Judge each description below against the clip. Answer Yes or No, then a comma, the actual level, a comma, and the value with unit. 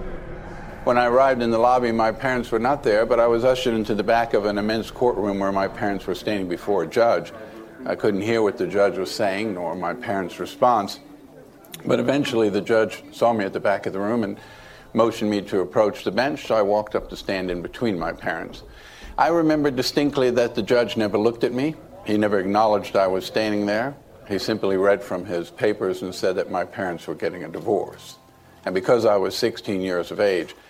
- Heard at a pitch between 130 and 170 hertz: No, low, 110 Hz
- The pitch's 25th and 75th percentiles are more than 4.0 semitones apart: No, average, 3.3 semitones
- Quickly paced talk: Yes, fast, 215 wpm